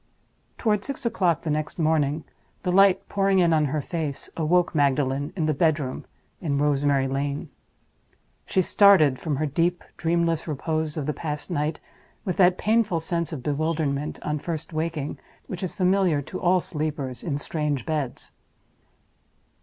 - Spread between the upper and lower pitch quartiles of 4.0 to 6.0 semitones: No, average, 3.2 semitones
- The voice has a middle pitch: Yes, medium, 155 Hz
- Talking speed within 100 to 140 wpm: No, average, 155 wpm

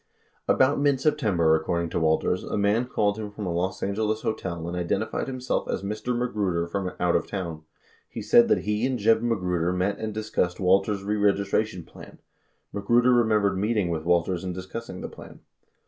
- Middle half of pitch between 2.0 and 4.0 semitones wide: Yes, average, 3.7 semitones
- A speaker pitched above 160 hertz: No, low, 100 Hz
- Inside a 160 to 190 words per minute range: Yes, average, 180 wpm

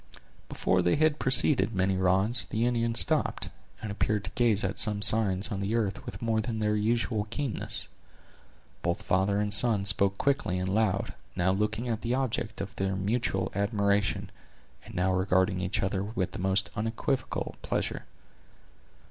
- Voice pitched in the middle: No, low, 105 Hz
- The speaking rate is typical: Yes, average, 165 wpm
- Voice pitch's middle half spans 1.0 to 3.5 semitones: Yes, average, 3.1 semitones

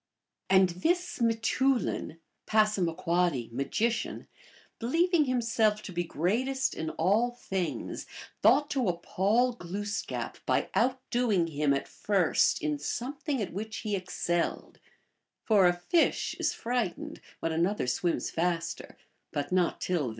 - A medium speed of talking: No, slow, 120 wpm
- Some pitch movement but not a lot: No, wide, 5.8 semitones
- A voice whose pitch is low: No, high, 200 Hz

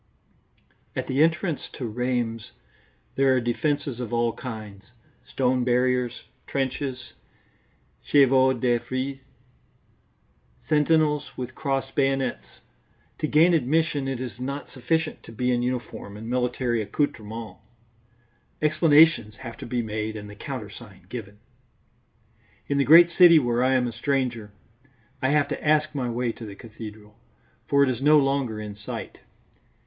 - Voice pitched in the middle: No, low, 125 Hz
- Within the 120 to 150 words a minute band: Yes, average, 140 wpm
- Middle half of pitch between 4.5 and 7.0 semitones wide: No, average, 3.4 semitones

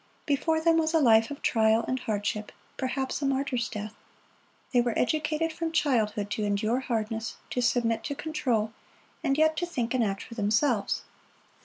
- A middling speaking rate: Yes, average, 170 wpm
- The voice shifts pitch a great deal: No, average, 5.0 semitones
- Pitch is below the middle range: No, high, 245 Hz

